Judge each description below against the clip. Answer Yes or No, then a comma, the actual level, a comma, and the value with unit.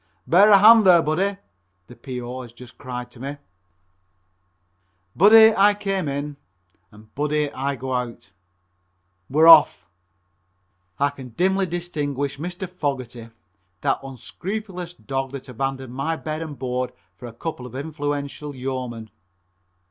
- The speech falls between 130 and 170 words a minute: Yes, slow, 135 wpm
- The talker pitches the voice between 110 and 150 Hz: Yes, medium, 140 Hz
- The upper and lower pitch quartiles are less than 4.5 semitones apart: No, wide, 5.4 semitones